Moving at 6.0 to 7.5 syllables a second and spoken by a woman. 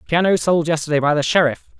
No: 6.7 syllables/s; male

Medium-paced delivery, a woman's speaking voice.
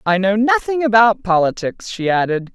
Yes: average, 165 wpm; female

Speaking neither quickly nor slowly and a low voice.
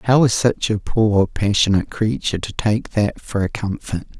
Yes: average, 185 wpm; low, 105 Hz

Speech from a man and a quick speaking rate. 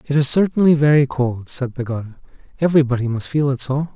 No: male; average, 180 wpm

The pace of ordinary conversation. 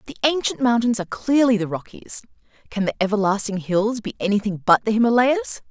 Yes: average, 170 wpm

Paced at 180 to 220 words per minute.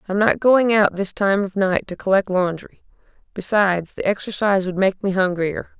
Yes: average, 185 wpm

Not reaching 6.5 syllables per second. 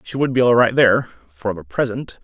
Yes: 5.9 syllables/s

